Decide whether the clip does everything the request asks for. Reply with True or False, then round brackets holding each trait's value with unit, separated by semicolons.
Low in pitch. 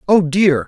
False (170 Hz)